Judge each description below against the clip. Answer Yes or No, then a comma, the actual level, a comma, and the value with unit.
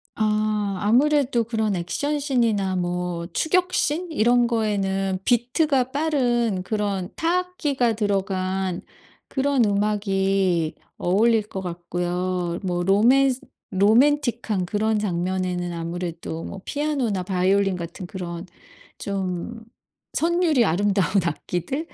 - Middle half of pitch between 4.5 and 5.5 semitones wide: Yes, average, 5.1 semitones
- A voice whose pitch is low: No, high, 205 Hz